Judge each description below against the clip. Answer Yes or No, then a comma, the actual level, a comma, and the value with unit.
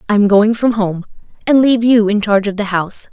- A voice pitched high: Yes, high, 210 Hz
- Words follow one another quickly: Yes, fast, 250 wpm